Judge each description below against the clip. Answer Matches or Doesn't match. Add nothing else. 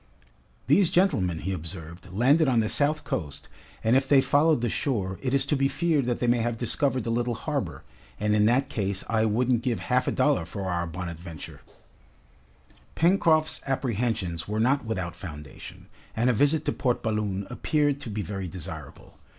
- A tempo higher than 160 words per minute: Matches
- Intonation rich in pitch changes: Matches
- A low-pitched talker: Matches